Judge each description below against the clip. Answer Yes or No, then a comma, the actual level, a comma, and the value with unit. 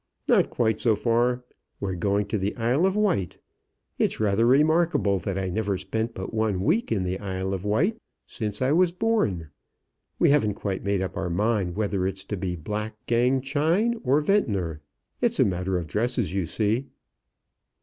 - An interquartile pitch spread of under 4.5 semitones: No, average, 5.1 semitones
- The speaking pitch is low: Yes, low, 105 Hz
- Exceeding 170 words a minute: Yes, average, 180 wpm